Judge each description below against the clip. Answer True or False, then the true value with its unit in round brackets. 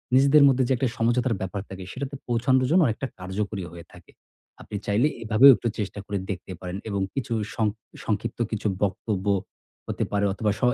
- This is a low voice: True (110 Hz)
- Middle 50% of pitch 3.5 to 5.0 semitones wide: True (4.5 semitones)